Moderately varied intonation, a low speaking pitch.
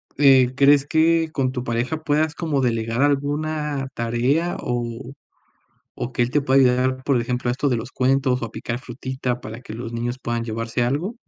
Yes: average, 3.1 semitones; low, 130 Hz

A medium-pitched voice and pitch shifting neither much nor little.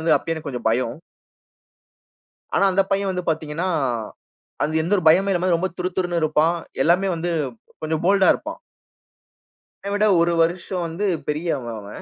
Yes: medium, 170 Hz; average, 3.0 semitones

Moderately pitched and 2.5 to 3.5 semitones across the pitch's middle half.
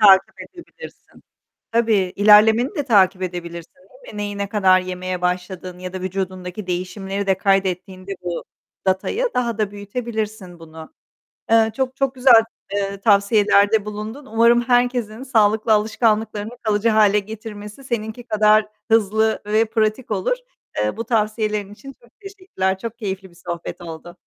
No: high, 210 Hz; average, 3.1 semitones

